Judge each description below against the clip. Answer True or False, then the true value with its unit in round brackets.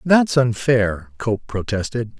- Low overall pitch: True (115 Hz)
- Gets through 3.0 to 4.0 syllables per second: True (3.6 syllables/s)